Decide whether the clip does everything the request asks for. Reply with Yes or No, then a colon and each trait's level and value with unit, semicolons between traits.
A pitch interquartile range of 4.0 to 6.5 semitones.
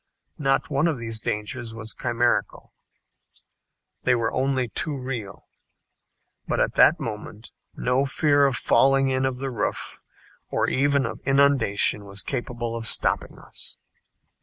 No: average, 3.1 semitones